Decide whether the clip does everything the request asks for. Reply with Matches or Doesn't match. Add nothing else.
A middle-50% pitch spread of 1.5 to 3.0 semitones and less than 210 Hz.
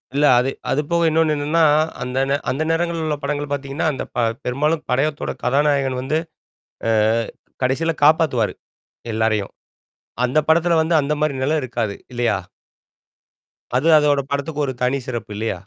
Doesn't match